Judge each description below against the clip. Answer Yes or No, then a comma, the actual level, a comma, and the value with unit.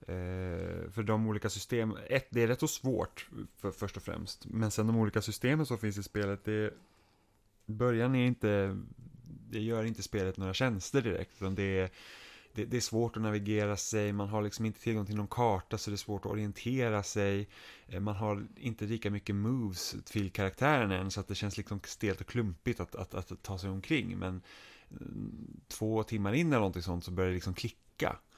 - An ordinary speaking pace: No, fast, 200 wpm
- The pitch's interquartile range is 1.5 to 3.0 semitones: Yes, narrow, 2.5 semitones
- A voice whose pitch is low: Yes, low, 105 Hz